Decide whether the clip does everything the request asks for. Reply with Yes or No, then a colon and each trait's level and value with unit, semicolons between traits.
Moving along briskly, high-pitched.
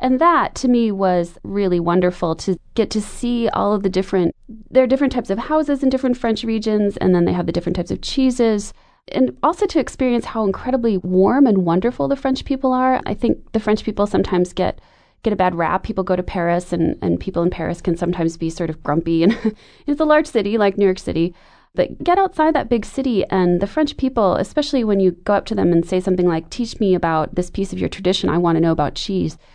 Yes: fast, 240 wpm; high, 205 Hz